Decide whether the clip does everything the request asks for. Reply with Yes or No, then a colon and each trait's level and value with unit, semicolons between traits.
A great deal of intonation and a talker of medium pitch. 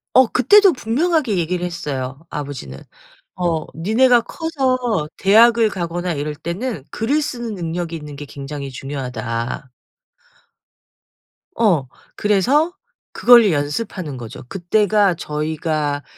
Yes: wide, 8.0 semitones; medium, 175 Hz